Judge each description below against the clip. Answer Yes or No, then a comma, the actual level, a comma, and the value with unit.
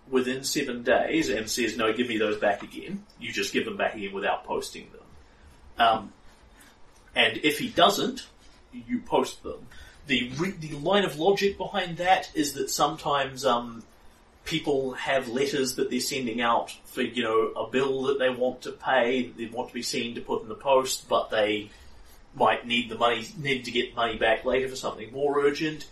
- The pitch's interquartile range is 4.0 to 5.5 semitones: Yes, average, 5.0 semitones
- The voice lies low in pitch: Yes, low, 130 Hz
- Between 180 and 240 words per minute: Yes, average, 195 wpm